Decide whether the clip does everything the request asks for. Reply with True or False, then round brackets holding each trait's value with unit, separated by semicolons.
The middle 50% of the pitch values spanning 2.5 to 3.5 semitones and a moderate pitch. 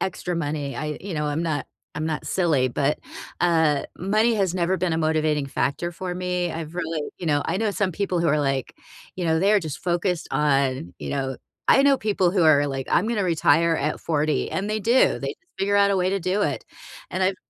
False (3.9 semitones; 170 Hz)